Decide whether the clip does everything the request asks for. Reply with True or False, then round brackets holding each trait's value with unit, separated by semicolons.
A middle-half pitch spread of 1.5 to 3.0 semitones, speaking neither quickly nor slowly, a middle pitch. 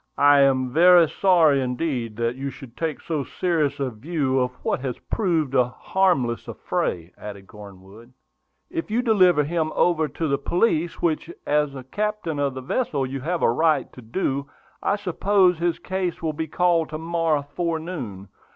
False (4.9 semitones; 170 wpm; 150 Hz)